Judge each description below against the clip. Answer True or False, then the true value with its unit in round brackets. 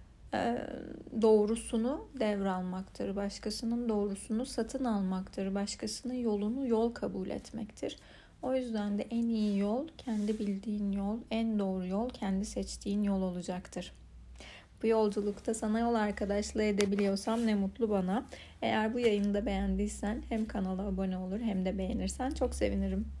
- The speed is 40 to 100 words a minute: False (130 wpm)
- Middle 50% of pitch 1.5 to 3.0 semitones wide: True (2.6 semitones)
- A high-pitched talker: True (210 Hz)